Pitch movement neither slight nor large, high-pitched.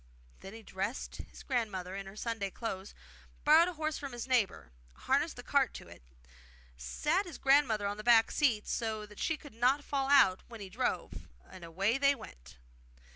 No: wide, 5.9 semitones; high, 225 Hz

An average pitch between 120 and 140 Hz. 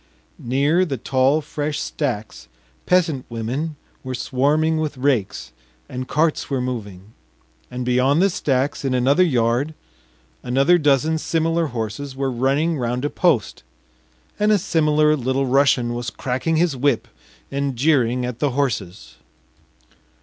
Yes: low, 135 Hz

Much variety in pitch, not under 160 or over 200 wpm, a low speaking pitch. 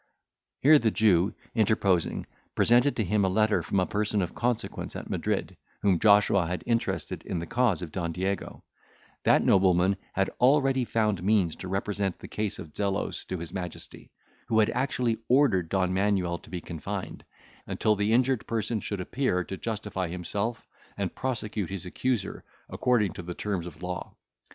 No: average, 3.7 semitones; average, 170 wpm; low, 100 Hz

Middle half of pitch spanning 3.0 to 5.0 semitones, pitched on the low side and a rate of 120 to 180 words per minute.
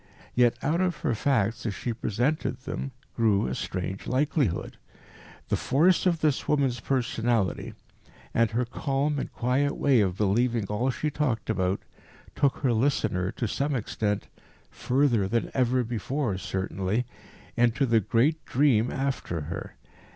Yes: average, 4.6 semitones; low, 120 Hz; average, 145 wpm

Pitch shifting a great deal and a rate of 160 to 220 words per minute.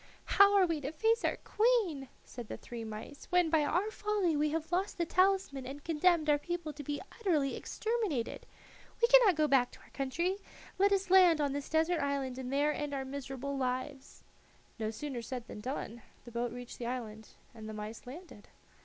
Yes: wide, 5.8 semitones; average, 195 wpm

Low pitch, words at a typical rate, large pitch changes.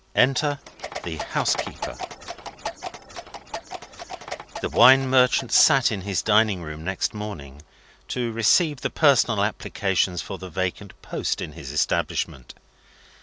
No: low, 105 Hz; slow, 115 wpm; wide, 5.9 semitones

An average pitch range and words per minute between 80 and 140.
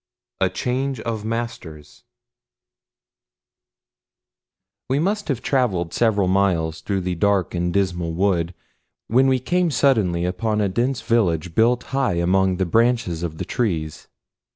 No: wide, 5.8 semitones; slow, 135 wpm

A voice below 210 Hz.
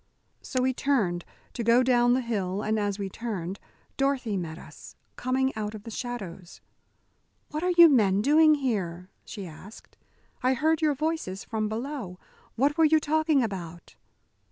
No: high, 235 Hz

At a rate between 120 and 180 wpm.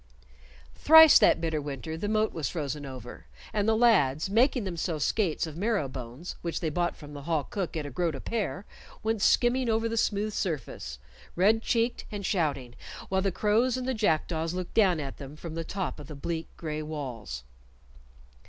No: average, 190 wpm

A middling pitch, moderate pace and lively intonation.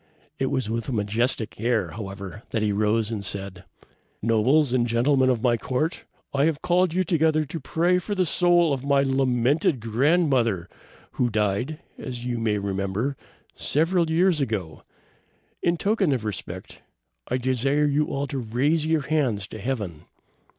No: low, 130 Hz; average, 160 wpm; wide, 5.8 semitones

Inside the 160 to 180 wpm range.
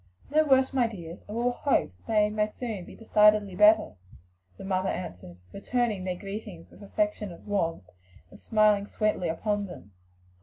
Yes: average, 165 wpm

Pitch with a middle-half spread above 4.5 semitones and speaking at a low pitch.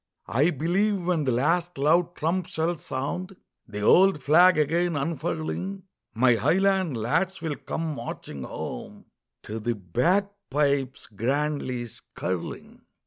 No: wide, 5.5 semitones; medium, 155 Hz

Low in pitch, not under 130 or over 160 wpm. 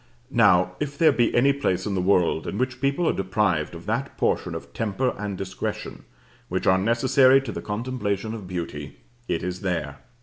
No: low, 105 Hz; average, 190 wpm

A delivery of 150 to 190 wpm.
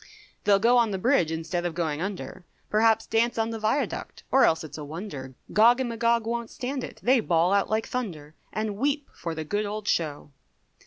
No: fast, 205 wpm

